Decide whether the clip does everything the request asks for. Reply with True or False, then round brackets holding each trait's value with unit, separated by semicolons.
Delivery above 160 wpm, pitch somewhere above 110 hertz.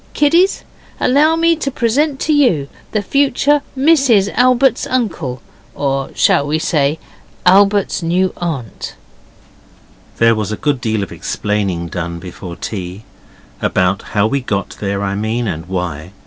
False (140 wpm; 140 Hz)